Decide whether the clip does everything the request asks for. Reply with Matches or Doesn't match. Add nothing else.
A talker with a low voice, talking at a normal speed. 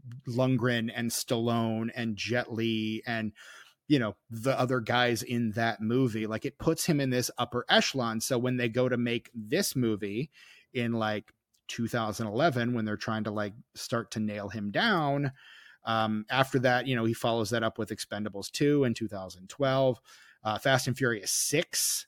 Matches